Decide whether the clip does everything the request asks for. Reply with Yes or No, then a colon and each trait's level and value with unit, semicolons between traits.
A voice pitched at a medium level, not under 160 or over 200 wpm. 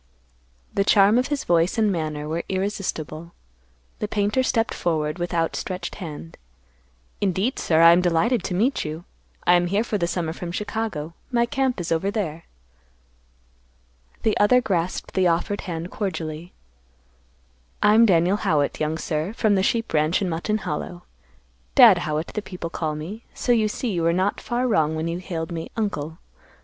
Yes: medium, 180 Hz; average, 170 wpm